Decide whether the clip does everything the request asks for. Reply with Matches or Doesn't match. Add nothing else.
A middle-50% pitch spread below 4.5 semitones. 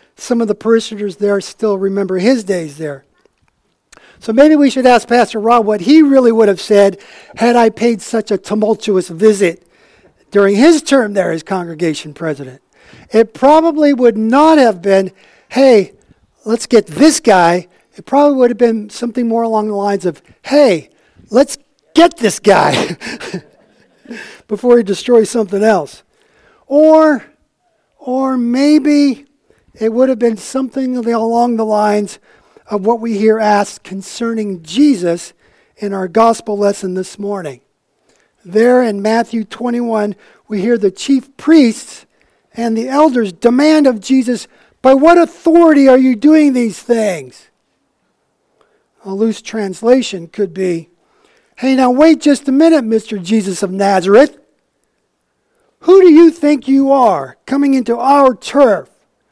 Doesn't match